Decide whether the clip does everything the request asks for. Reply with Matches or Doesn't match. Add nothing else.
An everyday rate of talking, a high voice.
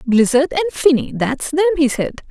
Matches